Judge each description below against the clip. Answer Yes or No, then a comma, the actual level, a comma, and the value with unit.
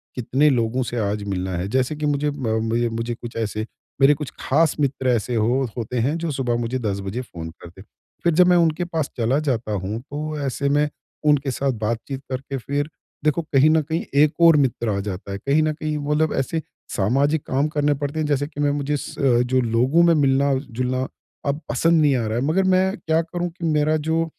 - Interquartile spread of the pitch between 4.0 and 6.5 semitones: Yes, average, 4.3 semitones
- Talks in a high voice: No, medium, 140 Hz